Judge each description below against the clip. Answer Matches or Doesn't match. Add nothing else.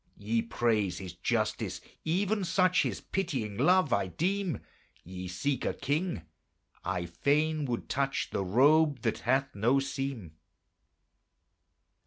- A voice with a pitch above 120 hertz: Matches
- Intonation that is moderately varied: Doesn't match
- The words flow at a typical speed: Doesn't match